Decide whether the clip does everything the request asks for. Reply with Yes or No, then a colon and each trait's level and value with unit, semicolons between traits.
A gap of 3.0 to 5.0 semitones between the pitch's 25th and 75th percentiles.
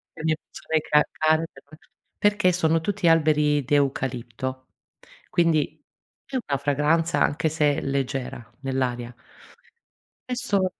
Yes: average, 3.4 semitones